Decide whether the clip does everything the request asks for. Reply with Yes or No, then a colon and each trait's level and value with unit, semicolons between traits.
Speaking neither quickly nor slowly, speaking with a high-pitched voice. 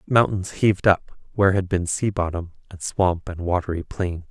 No: average, 180 wpm; very low, 95 Hz